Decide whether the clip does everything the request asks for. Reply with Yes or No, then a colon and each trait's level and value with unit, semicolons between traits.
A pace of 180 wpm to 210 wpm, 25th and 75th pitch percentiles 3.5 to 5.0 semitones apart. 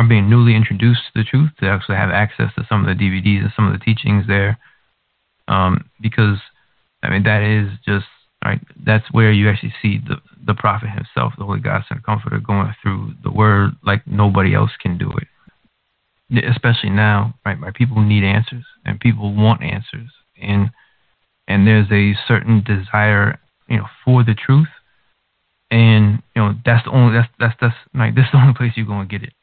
No: average, 195 wpm; average, 2.8 semitones